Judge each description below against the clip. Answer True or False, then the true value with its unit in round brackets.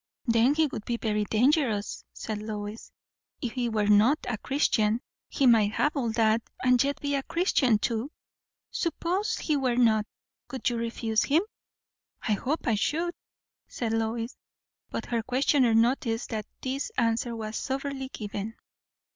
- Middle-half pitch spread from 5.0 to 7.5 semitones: False (3.8 semitones)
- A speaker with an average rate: True (155 wpm)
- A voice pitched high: True (235 Hz)